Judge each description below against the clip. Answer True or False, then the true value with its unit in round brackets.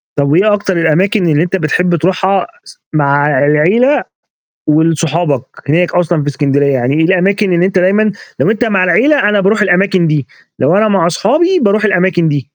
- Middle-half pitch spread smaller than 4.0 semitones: False (4.7 semitones)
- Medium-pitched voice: True (180 Hz)